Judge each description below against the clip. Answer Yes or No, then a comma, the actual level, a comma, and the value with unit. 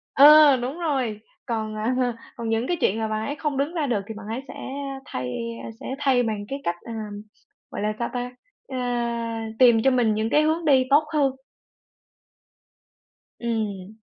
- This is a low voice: No, high, 245 Hz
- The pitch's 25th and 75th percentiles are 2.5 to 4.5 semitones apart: Yes, average, 4.2 semitones